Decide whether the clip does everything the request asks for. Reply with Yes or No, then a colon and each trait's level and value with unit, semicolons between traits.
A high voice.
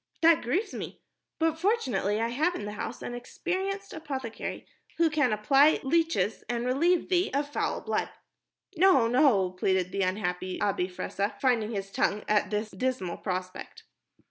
Yes: high, 245 Hz